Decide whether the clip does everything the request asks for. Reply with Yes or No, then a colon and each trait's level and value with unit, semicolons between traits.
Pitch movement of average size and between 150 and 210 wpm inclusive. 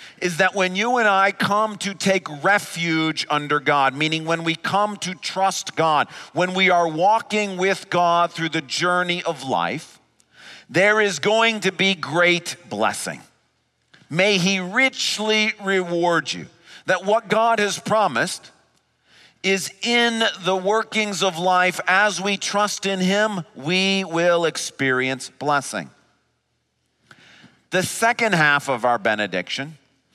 No: average, 4.3 semitones; slow, 135 wpm